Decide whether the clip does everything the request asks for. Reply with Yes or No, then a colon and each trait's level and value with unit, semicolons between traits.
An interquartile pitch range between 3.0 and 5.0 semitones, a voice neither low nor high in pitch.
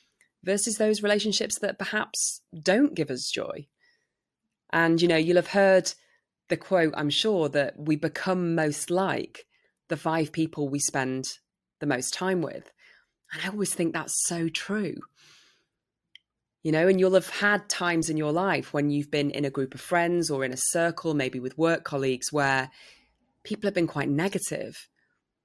Yes: average, 4.6 semitones; medium, 165 Hz